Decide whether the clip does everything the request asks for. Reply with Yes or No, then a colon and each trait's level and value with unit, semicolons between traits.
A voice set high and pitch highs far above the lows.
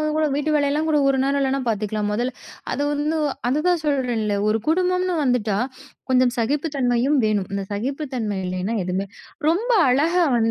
Yes: very high, 265 Hz; wide, 5.7 semitones